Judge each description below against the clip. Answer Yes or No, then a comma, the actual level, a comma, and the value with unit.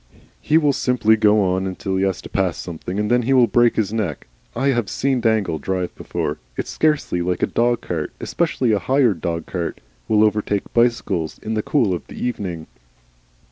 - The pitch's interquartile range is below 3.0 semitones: No, average, 4.8 semitones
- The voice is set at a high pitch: No, low, 105 Hz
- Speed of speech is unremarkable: Yes, average, 195 wpm